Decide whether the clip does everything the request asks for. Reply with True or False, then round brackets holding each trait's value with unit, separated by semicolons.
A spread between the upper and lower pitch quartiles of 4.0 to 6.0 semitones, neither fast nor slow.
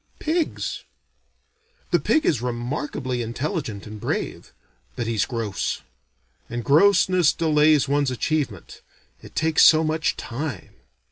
False (5.0 semitones; 115 wpm)